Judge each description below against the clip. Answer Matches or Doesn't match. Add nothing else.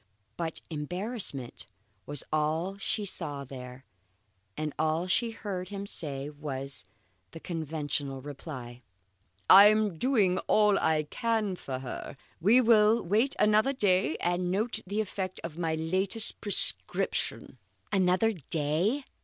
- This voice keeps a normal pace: Doesn't match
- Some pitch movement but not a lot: Doesn't match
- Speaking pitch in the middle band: Matches